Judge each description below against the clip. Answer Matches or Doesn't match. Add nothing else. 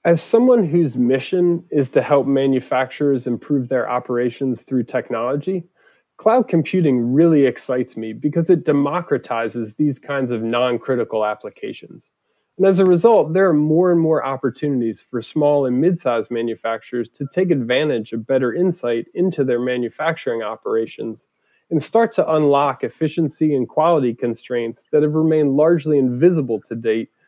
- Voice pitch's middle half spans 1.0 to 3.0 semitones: Doesn't match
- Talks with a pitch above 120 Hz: Matches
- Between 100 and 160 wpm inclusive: Matches